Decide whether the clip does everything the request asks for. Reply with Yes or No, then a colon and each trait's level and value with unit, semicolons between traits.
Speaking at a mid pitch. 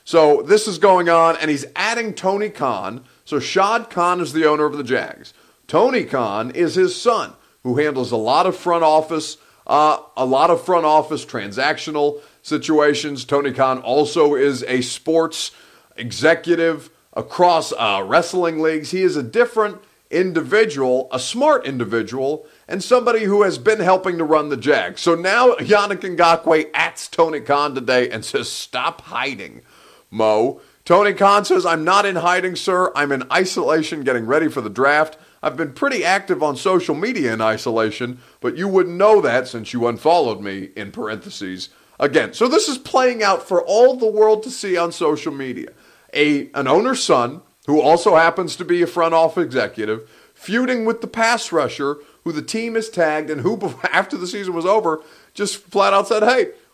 Yes: medium, 165 Hz